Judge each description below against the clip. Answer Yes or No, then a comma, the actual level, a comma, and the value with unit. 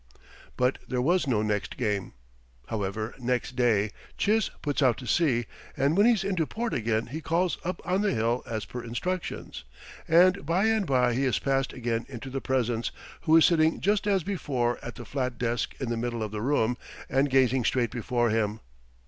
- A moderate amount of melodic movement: No, wide, 5.7 semitones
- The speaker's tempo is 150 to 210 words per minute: Yes, average, 190 wpm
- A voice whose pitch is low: Yes, low, 125 Hz